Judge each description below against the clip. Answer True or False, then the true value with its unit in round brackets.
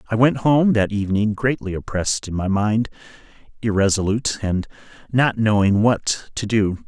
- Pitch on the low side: True (105 Hz)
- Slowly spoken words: False (150 wpm)